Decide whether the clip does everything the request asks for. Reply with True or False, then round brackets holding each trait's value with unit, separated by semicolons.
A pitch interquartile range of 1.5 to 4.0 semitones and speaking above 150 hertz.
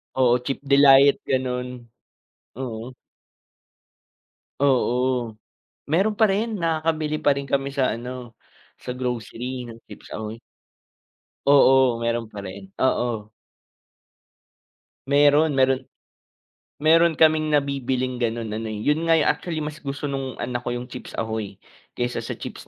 False (3.4 semitones; 130 Hz)